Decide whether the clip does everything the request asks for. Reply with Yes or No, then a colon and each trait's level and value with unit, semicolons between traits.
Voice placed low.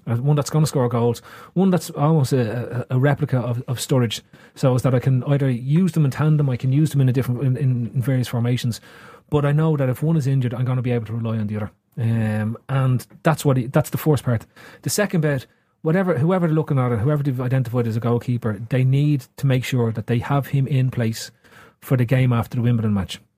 Yes: low, 130 Hz